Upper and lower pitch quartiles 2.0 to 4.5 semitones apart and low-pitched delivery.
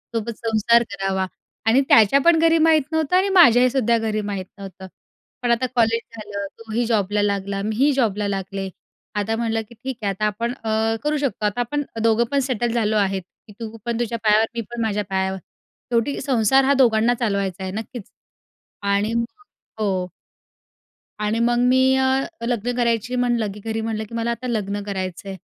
No: average, 2.9 semitones; high, 225 Hz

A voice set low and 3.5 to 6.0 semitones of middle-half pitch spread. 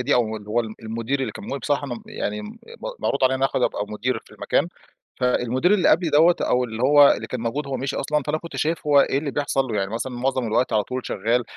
Yes: low, 130 Hz; average, 4.0 semitones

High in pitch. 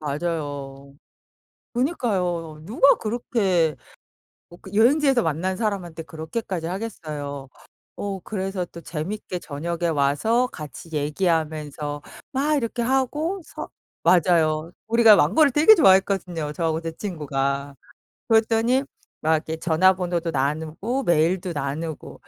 No: medium, 175 Hz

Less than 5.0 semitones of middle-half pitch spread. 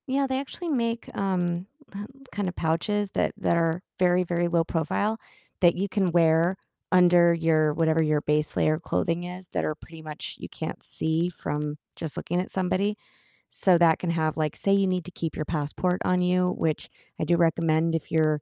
Yes: narrow, 2.4 semitones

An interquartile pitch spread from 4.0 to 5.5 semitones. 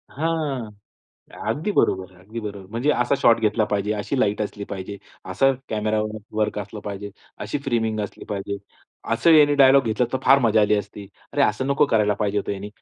Yes: average, 4.3 semitones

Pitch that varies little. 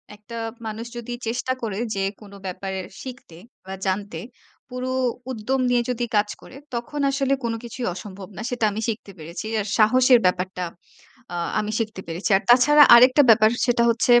No: average, 3.7 semitones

